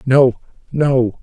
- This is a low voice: Yes, low, 130 Hz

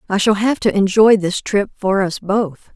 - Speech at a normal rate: No, fast, 220 wpm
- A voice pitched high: Yes, high, 200 Hz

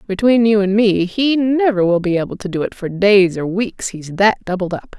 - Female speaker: Yes, female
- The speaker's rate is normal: No, fast, 240 wpm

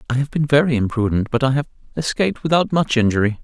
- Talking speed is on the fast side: Yes, fast, 210 wpm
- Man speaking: Yes, male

